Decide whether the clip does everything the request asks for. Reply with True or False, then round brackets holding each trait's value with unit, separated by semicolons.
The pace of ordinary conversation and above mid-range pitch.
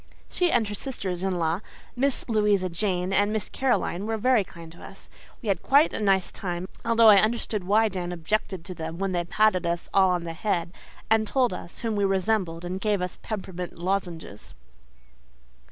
True (190 wpm; 195 Hz)